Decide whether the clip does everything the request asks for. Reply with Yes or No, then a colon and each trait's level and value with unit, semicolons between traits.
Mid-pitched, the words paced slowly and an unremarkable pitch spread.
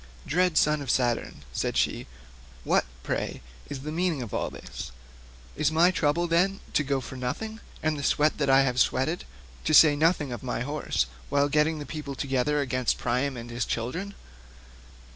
No: medium, 145 Hz; average, 180 wpm; average, 3.6 semitones